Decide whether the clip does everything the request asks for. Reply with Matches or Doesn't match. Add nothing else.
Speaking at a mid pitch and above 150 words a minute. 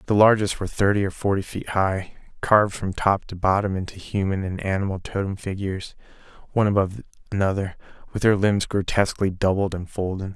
Doesn't match